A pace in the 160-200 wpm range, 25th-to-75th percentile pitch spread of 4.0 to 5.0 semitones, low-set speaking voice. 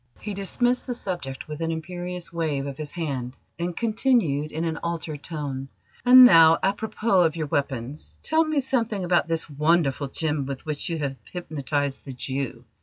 No: average, 170 wpm; average, 4.5 semitones; medium, 160 Hz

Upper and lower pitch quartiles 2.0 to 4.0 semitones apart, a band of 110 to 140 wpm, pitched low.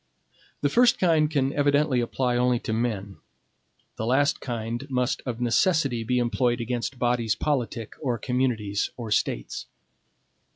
Yes: average, 3.0 semitones; slow, 135 wpm; low, 125 Hz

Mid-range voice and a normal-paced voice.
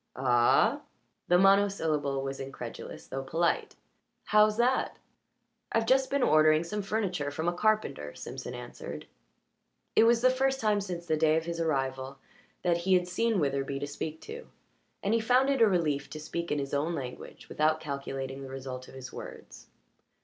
Yes: medium, 165 Hz; average, 175 wpm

